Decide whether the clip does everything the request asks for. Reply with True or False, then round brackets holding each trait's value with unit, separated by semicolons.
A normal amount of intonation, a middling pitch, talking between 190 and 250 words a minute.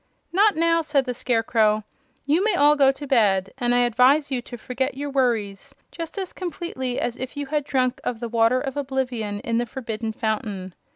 False (4.0 semitones; 255 Hz; 195 wpm)